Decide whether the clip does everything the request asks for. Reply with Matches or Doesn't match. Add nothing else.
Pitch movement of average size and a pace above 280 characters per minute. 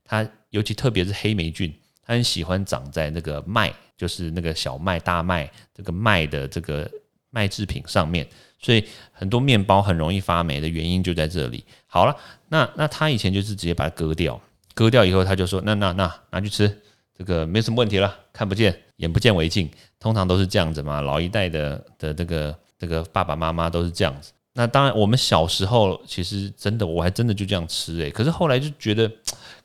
Matches